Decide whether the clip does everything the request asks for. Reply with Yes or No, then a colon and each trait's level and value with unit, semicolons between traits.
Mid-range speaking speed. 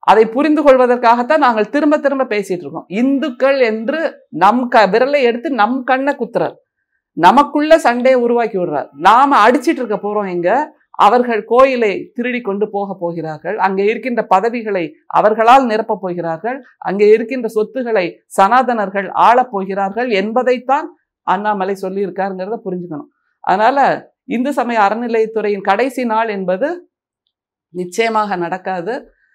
Yes: average, 115 wpm